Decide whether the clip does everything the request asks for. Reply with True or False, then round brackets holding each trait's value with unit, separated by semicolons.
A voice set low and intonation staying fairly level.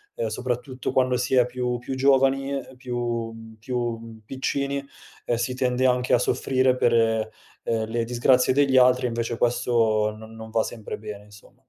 True (125 Hz; 2.2 semitones)